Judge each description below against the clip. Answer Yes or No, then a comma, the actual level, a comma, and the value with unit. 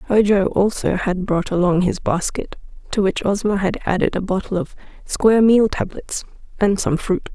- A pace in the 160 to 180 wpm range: Yes, average, 170 wpm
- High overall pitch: Yes, high, 195 Hz